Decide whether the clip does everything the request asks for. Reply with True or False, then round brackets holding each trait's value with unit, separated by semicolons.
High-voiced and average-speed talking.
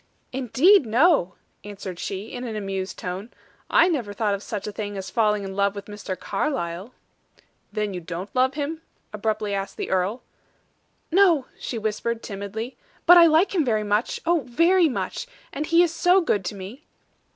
True (220 Hz; 175 wpm)